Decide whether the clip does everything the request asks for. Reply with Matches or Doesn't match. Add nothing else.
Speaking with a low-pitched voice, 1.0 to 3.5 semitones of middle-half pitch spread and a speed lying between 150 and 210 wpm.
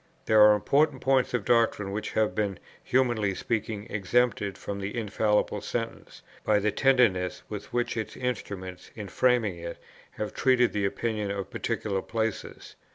Matches